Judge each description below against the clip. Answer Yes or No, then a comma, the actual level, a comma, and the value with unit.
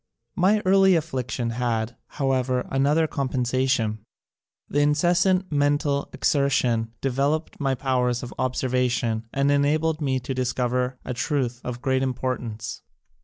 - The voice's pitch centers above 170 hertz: No, low, 130 Hz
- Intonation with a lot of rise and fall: No, average, 2.8 semitones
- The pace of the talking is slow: Yes, slow, 120 wpm